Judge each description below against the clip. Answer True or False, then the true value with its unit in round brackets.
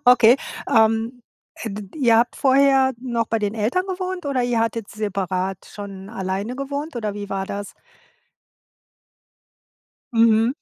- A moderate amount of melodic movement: True (4.1 semitones)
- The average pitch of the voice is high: True (225 Hz)